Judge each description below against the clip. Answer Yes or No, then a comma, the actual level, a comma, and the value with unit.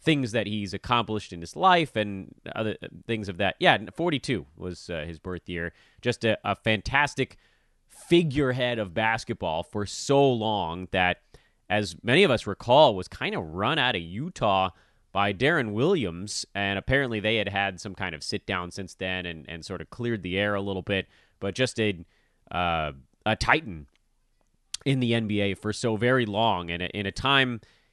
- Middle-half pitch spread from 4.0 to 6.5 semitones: Yes, average, 4.3 semitones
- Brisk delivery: No, average, 180 wpm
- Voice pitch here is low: Yes, low, 105 Hz